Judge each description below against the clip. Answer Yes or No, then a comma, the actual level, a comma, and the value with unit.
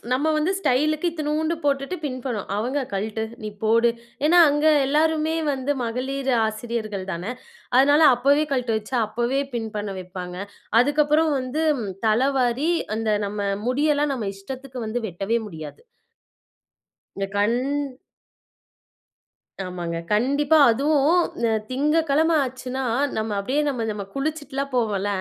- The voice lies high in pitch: Yes, very high, 260 Hz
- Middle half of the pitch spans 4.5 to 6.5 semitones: Yes, average, 5.2 semitones